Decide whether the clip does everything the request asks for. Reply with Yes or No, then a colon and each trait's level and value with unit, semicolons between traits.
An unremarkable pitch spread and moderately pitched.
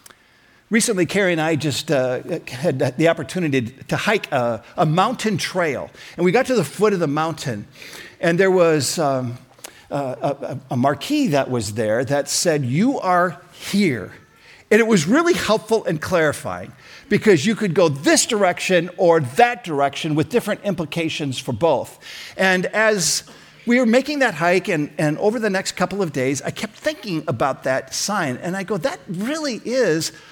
No: wide, 6.0 semitones; medium, 175 Hz